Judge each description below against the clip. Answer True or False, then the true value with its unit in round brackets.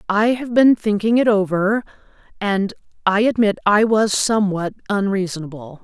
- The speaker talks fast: False (135 wpm)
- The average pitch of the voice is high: True (205 Hz)